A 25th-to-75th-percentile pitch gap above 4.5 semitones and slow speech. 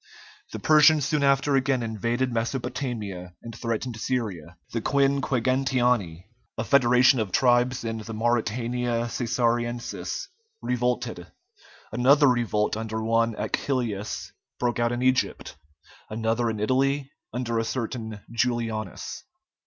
No: narrow, 2.4 semitones; slow, 115 wpm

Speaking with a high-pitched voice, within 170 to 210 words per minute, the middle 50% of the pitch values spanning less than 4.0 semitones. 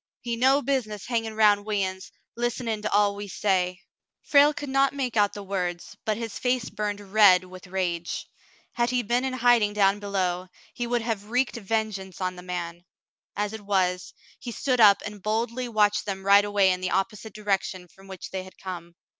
Yes: high, 205 Hz; average, 200 wpm; average, 3.6 semitones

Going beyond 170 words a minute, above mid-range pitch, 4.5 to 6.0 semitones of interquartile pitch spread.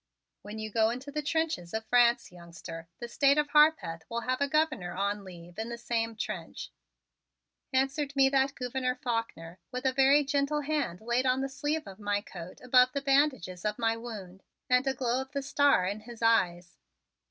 Yes: average, 190 wpm; high, 245 Hz; average, 5.0 semitones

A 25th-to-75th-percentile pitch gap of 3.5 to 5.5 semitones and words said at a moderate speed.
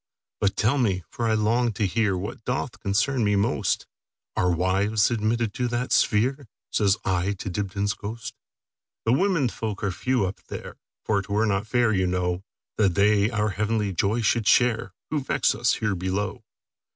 No: average, 3.0 semitones; average, 150 wpm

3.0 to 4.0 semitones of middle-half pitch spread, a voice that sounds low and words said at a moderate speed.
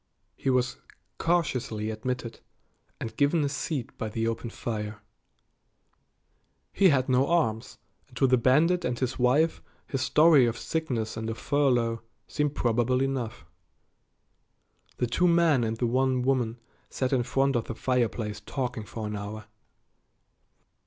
Yes: average, 3.3 semitones; low, 125 Hz; average, 145 wpm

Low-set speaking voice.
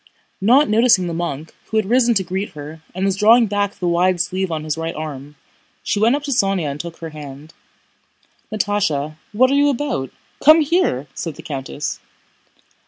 No: medium, 185 Hz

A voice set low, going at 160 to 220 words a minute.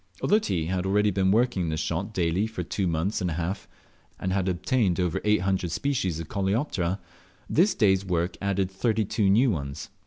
Yes: very low, 95 Hz; average, 180 wpm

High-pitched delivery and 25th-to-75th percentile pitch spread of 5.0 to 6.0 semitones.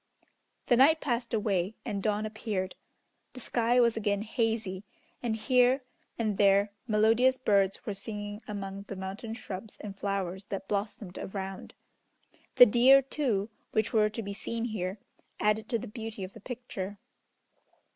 No: high, 215 Hz; average, 2.8 semitones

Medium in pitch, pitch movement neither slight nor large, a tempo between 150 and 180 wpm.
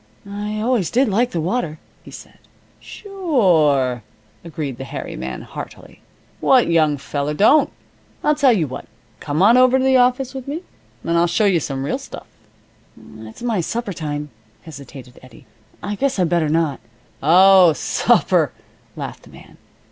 No: medium, 175 Hz; wide, 8.7 semitones; average, 165 wpm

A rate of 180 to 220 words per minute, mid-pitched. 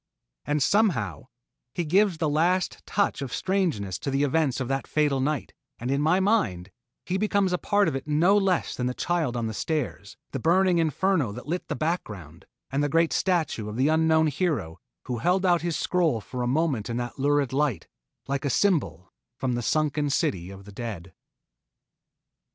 Yes: average, 190 wpm; medium, 150 Hz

